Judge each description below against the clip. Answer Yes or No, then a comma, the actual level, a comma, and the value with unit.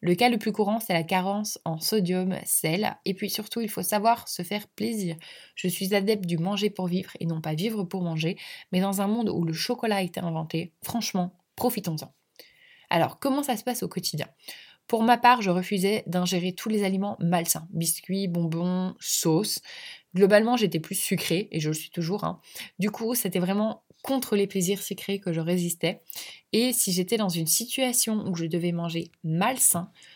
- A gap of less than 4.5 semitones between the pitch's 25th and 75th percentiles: Yes, average, 3.9 semitones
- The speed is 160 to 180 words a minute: No, average, 195 wpm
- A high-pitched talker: Yes, high, 195 Hz